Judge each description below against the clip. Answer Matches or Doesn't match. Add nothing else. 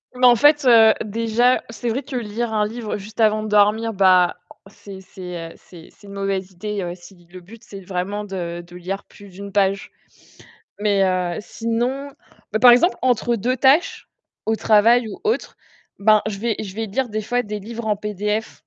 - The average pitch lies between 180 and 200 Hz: Doesn't match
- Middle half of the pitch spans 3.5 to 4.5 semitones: Doesn't match